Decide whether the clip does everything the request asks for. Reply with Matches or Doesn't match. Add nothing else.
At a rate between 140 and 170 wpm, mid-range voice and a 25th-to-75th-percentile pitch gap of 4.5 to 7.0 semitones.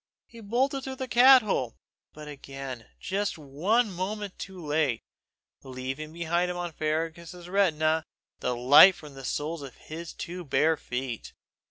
Matches